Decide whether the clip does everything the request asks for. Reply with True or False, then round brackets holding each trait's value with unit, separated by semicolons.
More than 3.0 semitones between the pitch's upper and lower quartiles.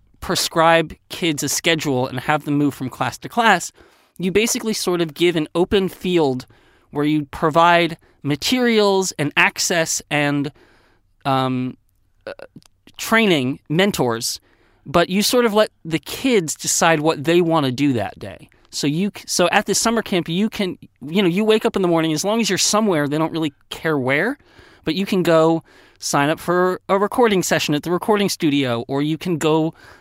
True (4.8 semitones)